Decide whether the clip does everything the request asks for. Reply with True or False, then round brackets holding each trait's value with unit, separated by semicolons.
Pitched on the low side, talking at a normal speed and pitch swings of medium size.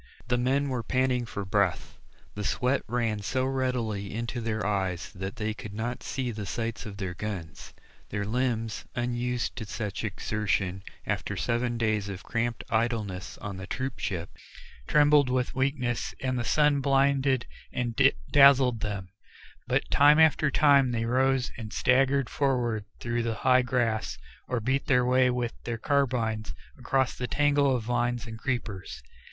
True (120 Hz; 160 wpm; 3.3 semitones)